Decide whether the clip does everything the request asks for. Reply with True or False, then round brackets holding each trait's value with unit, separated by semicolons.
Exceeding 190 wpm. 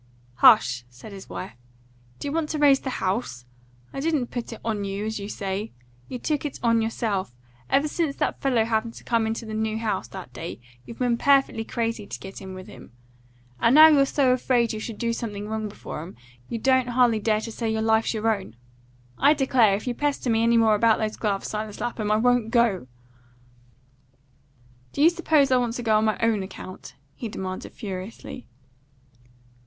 True (200 wpm)